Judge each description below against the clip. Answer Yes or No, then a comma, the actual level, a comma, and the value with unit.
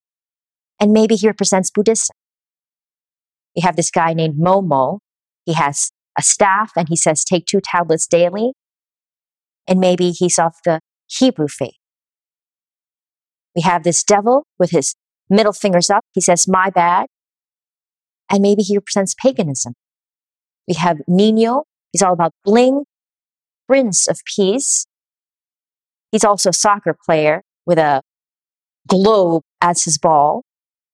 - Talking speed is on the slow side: Yes, slow, 130 wpm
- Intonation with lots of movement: No, average, 3.7 semitones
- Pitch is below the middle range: No, medium, 185 Hz